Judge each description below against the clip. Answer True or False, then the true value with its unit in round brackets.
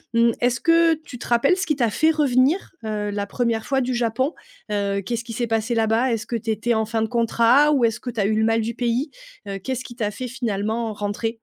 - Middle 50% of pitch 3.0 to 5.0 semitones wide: False (2.6 semitones)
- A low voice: False (235 Hz)